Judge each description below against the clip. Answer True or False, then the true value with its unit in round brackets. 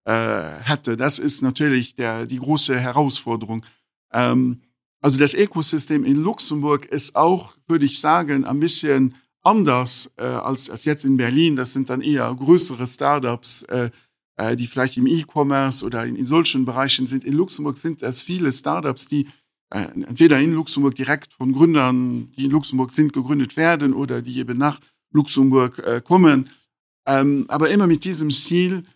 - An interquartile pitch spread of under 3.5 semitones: True (2.9 semitones)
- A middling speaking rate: True (160 wpm)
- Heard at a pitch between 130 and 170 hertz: True (140 Hz)